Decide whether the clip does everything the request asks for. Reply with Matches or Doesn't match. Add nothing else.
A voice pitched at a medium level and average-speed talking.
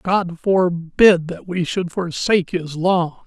Matches